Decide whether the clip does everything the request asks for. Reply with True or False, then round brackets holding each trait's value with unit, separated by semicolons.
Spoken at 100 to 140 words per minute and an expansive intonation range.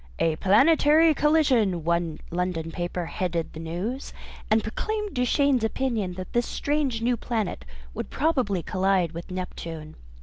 True (135 wpm; 7.4 semitones)